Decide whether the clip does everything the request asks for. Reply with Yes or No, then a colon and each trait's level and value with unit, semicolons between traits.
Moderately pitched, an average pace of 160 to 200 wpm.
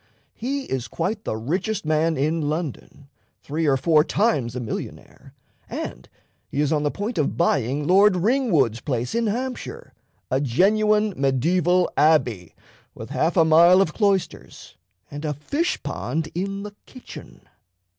No: medium, 165 Hz; average, 145 wpm